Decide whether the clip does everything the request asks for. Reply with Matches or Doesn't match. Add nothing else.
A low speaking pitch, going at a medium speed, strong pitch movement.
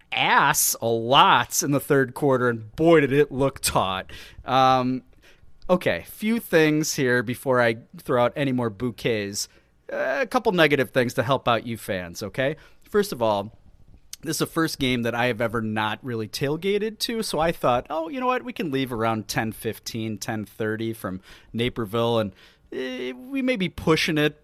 Matches